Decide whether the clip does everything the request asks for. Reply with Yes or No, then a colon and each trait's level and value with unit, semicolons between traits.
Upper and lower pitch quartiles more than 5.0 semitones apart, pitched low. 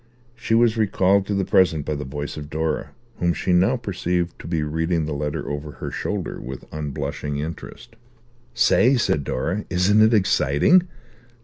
Yes: wide, 5.6 semitones; very low, 85 Hz